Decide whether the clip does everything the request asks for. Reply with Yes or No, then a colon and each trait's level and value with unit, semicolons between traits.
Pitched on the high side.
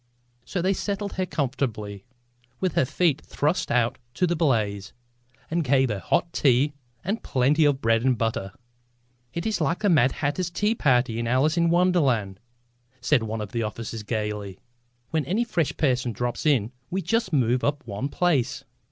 No: low, 135 Hz